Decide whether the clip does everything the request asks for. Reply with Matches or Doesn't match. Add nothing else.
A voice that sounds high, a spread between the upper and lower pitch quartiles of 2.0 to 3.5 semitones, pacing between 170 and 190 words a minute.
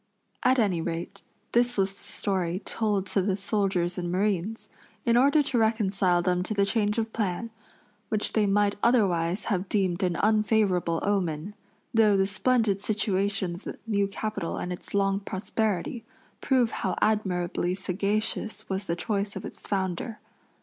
Doesn't match